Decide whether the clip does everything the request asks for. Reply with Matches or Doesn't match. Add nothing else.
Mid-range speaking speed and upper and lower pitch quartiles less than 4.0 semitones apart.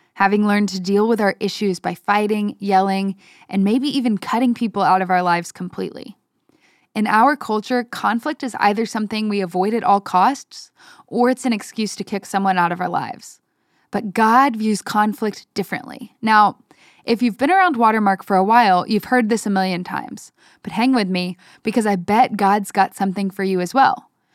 Matches